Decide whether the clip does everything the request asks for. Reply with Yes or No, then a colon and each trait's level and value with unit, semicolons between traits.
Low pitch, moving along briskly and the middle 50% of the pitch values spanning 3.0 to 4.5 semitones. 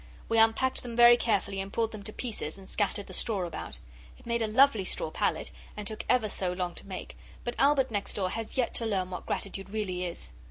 No: high, 215 Hz; fast, 230 wpm; average, 3.4 semitones